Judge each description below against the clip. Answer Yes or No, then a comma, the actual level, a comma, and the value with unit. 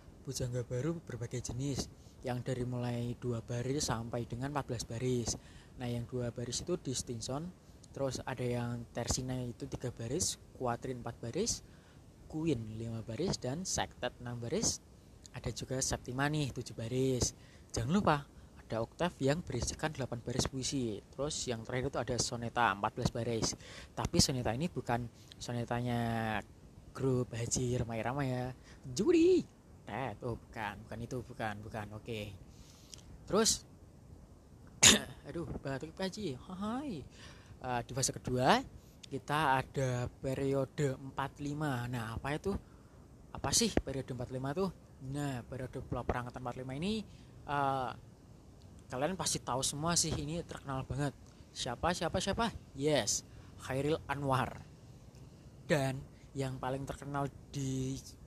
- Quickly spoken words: No, average, 125 wpm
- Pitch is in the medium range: No, low, 125 Hz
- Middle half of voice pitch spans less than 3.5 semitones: Yes, average, 2.8 semitones